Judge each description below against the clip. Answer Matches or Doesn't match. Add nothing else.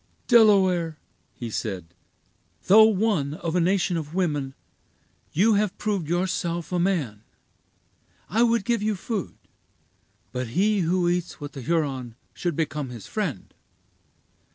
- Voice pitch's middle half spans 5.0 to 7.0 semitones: Matches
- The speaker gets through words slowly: Matches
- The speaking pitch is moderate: Matches